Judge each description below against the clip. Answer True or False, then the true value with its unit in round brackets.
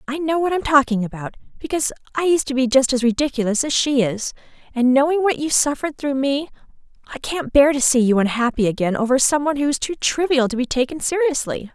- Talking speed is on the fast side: True (225 wpm)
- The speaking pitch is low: False (270 Hz)